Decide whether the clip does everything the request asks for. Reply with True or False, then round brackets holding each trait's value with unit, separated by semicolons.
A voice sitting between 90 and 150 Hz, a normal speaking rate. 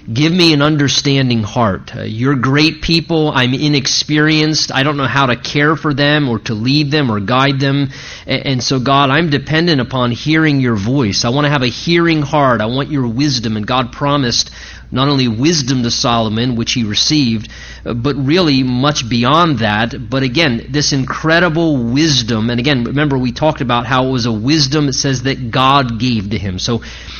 True (135 Hz; 190 wpm)